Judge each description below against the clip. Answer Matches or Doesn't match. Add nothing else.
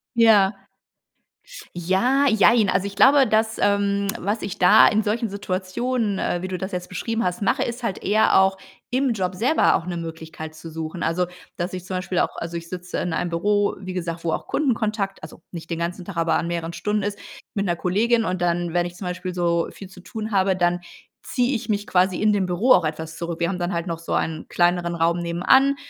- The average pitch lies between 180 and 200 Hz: Matches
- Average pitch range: Matches